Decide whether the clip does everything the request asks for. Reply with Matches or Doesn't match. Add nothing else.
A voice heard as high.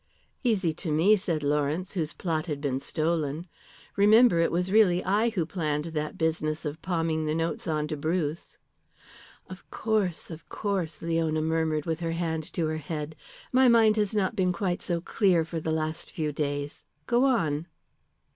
Doesn't match